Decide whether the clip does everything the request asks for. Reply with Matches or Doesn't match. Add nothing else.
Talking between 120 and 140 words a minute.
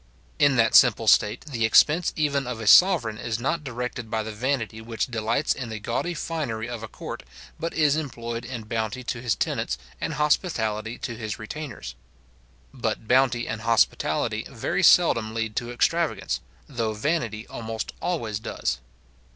Doesn't match